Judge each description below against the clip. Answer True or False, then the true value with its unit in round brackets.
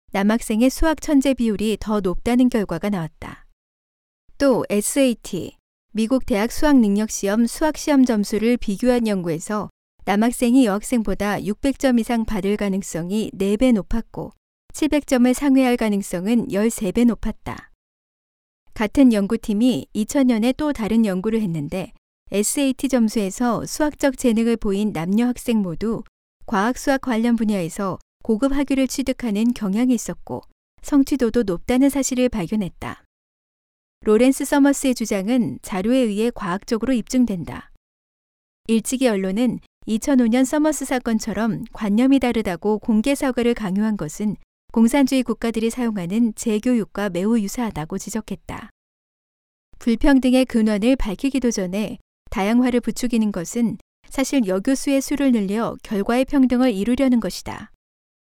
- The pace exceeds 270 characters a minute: True (300 characters per minute)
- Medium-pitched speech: False (230 Hz)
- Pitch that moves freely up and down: False (3.6 semitones)